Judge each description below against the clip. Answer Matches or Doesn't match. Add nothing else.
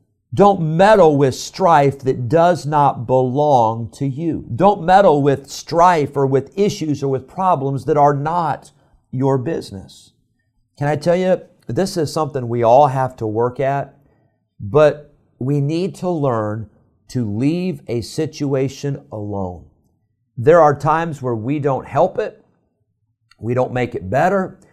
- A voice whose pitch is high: Doesn't match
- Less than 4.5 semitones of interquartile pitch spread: Doesn't match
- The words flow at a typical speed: Matches